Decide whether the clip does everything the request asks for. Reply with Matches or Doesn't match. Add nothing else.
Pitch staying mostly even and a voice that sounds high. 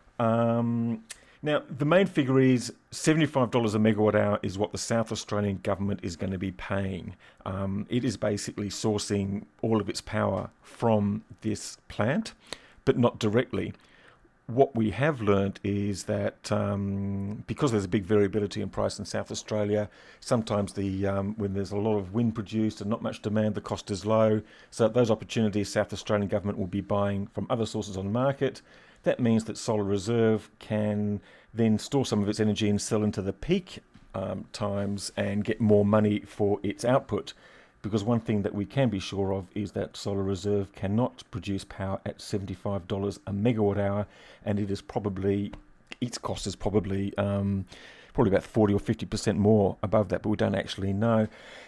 Doesn't match